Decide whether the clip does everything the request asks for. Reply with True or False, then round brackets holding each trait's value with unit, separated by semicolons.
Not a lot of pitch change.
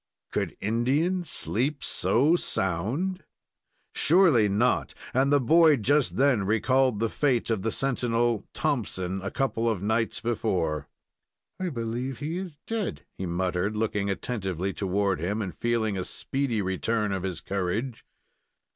False (5.6 semitones)